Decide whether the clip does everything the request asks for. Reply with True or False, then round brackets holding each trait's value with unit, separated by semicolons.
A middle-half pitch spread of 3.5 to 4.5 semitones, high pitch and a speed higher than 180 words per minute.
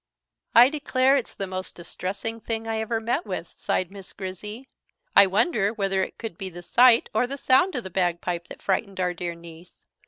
True (4.1 semitones; 200 Hz; 195 wpm)